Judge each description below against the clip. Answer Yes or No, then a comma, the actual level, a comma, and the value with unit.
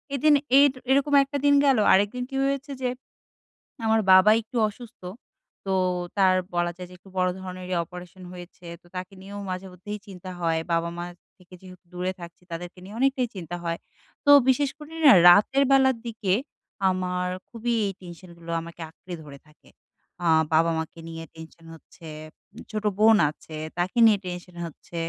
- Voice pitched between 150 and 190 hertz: Yes, medium, 185 Hz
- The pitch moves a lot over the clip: No, average, 4.4 semitones